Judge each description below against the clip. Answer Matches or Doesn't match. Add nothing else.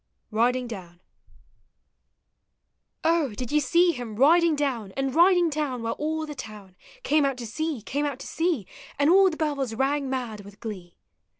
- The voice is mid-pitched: Doesn't match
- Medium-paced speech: Matches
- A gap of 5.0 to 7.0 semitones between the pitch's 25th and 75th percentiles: Matches